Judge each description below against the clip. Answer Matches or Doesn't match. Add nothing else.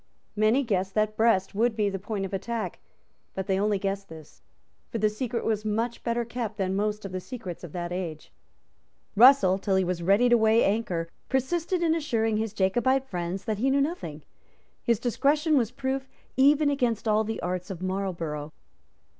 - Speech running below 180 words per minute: Doesn't match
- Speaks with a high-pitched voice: Matches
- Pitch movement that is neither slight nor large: Matches